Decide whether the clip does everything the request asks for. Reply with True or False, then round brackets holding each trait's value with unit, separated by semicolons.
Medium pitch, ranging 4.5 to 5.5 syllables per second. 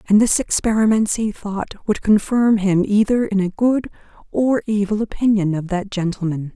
False (210 Hz; 4.8 syllables/s)